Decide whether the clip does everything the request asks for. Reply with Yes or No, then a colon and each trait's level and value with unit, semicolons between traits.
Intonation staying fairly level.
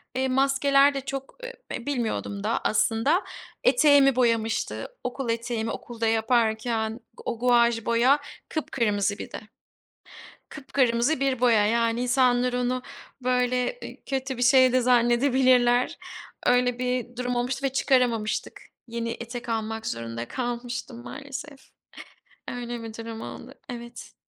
Yes: narrow, 2.1 semitones